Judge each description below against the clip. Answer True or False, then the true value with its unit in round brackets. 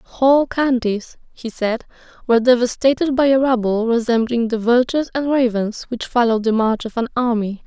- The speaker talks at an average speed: True (165 wpm)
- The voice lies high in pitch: True (240 Hz)